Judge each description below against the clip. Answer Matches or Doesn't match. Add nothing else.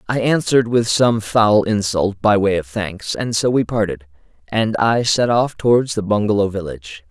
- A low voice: Matches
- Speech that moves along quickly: Doesn't match